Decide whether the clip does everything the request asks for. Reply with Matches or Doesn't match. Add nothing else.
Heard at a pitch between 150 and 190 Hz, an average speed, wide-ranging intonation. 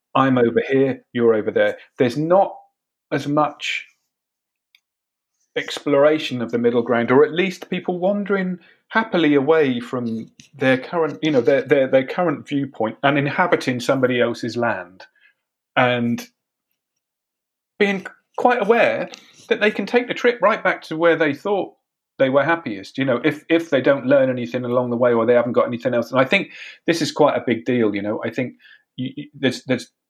Doesn't match